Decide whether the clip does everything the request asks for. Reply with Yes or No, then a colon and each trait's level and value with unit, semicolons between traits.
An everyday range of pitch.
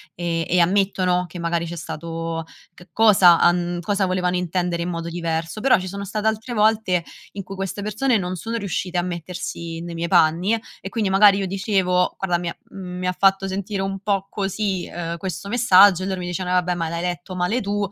No: narrow, 2.3 semitones